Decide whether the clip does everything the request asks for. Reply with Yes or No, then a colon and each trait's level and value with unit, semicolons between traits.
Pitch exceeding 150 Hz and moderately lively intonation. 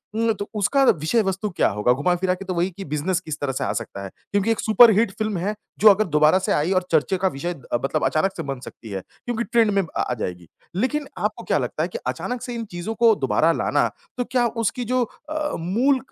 No: high, 190 Hz; wide, 6.6 semitones